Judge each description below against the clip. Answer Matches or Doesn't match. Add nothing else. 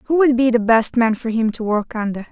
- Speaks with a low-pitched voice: Doesn't match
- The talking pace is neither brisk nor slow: Doesn't match